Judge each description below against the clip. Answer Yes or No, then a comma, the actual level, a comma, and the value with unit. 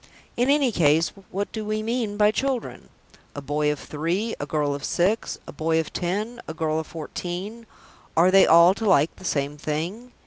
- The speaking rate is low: No, average, 195 wpm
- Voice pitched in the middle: Yes, medium, 175 Hz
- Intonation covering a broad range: Yes, wide, 5.7 semitones